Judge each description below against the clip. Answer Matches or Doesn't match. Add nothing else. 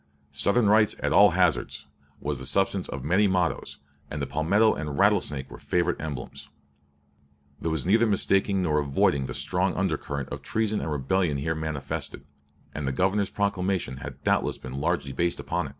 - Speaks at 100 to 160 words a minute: Doesn't match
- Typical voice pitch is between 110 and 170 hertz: Doesn't match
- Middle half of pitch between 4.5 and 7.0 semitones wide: Matches